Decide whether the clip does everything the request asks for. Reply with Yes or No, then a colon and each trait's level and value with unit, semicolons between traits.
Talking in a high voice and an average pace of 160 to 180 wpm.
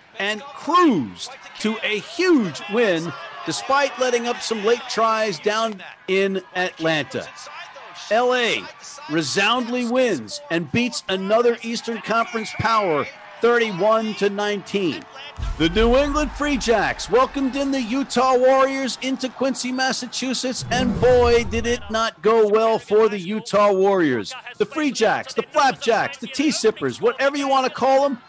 No: high, 230 Hz; average, 140 wpm